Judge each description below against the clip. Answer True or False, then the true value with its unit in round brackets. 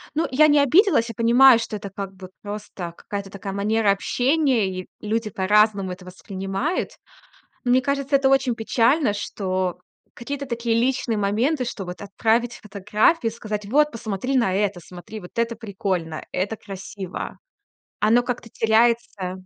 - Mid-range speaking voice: False (220 Hz)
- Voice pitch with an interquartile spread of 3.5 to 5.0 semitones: True (4.0 semitones)